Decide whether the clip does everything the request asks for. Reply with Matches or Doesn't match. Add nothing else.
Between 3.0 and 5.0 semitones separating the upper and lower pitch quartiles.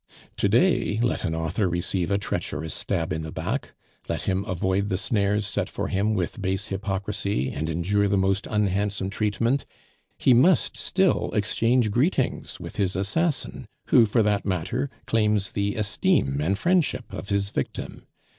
Doesn't match